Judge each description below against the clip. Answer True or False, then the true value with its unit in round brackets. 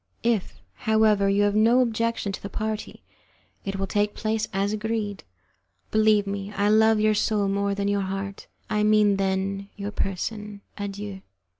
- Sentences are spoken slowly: False (160 wpm)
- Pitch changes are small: True (1.5 semitones)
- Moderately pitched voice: False (205 Hz)